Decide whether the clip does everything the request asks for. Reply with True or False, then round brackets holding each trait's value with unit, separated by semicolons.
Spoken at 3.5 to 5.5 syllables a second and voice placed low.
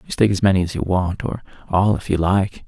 False (5.9 syllables/s; 95 Hz)